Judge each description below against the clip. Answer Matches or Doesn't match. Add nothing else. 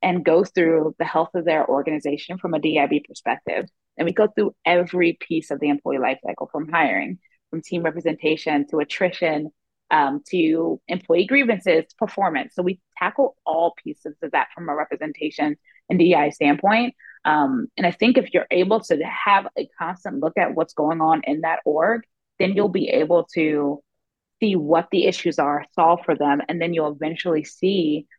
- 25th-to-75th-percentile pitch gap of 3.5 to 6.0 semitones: Doesn't match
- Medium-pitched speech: Matches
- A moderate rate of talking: Matches